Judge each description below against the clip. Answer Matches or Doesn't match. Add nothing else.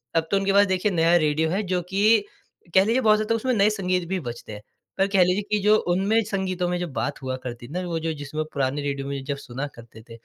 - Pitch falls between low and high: Matches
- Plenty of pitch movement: Matches